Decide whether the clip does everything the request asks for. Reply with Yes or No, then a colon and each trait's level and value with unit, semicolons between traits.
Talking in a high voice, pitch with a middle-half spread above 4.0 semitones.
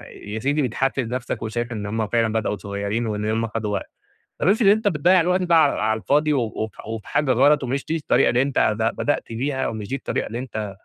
No: low, 120 Hz; average, 4.9 semitones